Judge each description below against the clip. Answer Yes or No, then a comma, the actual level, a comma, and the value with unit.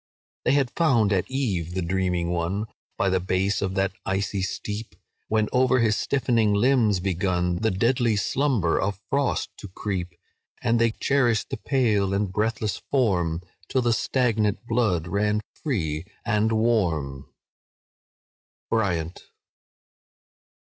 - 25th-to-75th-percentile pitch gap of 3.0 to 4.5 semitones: Yes, average, 4.2 semitones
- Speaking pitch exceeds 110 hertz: No, low, 105 Hz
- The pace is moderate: No, slow, 125 wpm